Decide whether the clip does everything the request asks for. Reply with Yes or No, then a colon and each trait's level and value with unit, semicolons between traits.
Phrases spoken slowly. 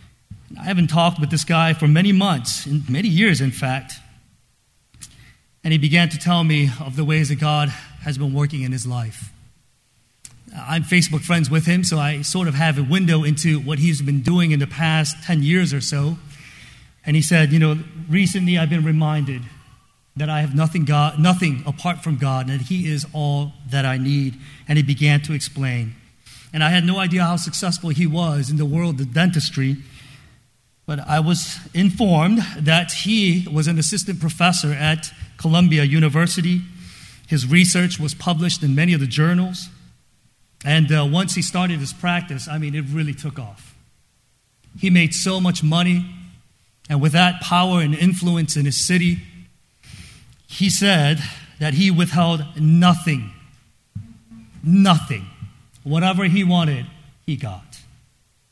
No: average, 165 wpm